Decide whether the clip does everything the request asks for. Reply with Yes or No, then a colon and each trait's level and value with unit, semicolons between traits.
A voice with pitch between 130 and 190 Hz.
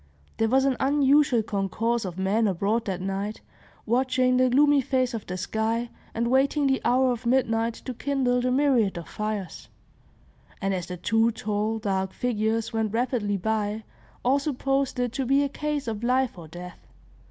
No: high, 230 Hz